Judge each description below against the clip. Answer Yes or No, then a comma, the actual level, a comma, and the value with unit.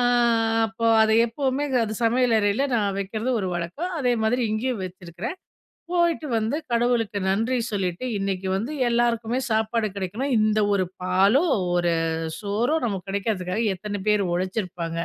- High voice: Yes, high, 215 Hz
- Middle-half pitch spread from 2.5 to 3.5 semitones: No, average, 3.9 semitones